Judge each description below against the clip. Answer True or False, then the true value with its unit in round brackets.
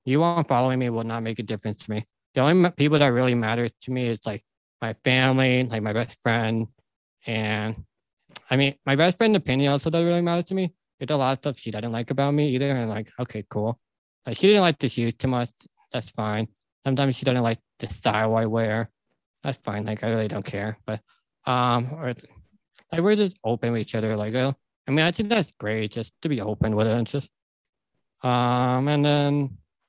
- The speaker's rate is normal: False (215 wpm)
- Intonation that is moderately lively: True (4.0 semitones)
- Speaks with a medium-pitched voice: False (125 Hz)